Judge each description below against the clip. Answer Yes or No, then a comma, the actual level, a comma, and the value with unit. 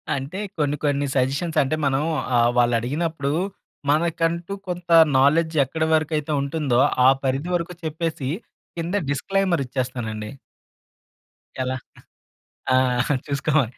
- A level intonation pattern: No, average, 3.9 semitones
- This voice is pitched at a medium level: Yes, medium, 145 Hz